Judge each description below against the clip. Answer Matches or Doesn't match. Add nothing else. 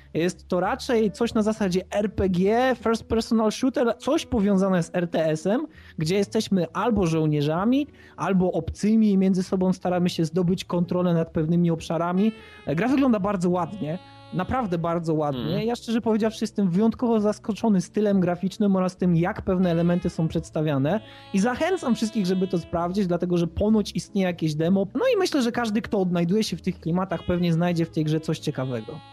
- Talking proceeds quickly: Matches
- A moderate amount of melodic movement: Matches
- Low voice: Doesn't match